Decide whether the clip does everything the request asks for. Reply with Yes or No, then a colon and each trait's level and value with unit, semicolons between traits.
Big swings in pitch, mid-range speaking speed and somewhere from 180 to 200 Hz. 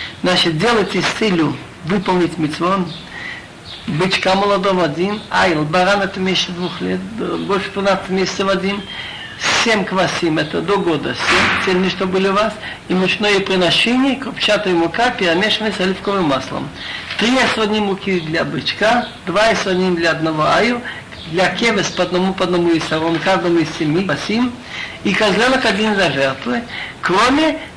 No: average, 3.4 semitones; average, 150 wpm; high, 190 Hz